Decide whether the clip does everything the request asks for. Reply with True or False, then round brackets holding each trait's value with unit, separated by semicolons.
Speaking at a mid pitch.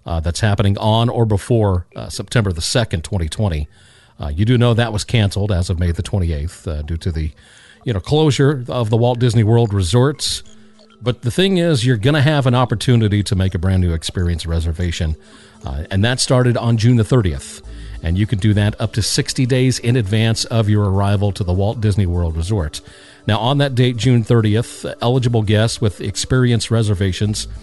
False (110 Hz)